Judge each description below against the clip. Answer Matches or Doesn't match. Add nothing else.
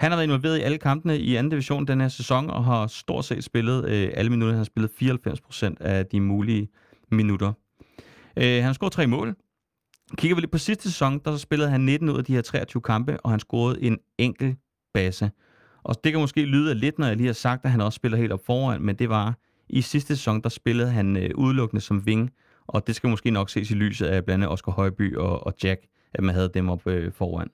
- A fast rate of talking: Matches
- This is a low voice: Matches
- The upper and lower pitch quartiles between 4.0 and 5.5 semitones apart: Matches